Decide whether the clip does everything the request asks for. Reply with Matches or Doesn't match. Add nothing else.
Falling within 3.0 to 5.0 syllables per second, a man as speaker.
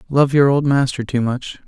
Matches